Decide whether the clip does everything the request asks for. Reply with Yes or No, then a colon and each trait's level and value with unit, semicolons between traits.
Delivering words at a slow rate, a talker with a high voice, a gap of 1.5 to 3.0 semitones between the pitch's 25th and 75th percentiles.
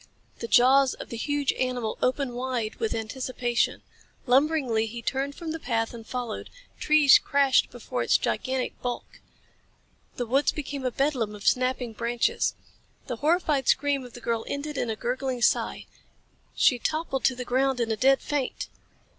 No: average, 165 wpm; very high, 255 Hz; average, 2.7 semitones